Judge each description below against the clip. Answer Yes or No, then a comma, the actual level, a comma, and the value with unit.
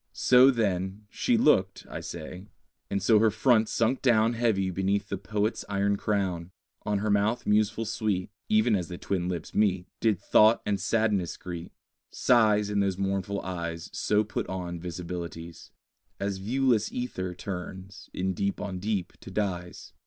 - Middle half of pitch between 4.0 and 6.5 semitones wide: No, average, 2.9 semitones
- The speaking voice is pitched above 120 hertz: No, low, 100 Hz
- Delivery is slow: No, average, 160 wpm